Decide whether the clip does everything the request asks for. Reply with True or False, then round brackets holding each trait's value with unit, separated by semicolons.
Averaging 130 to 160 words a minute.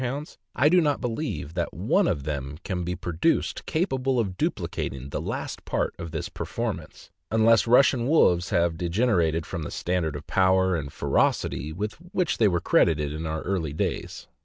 False (175 wpm)